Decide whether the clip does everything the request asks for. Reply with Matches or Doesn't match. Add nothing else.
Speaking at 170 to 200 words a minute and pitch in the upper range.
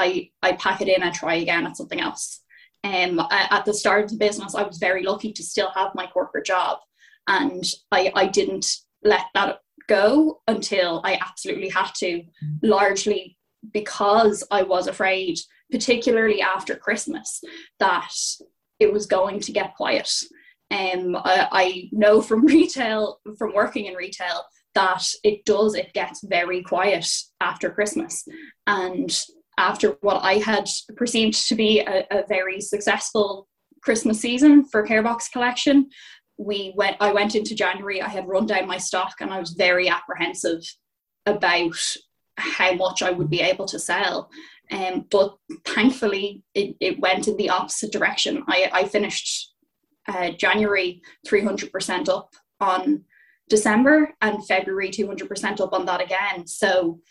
Doesn't match